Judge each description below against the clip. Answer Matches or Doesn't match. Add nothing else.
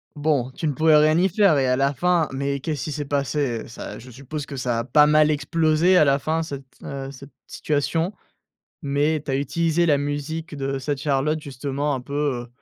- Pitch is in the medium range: Matches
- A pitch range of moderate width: Doesn't match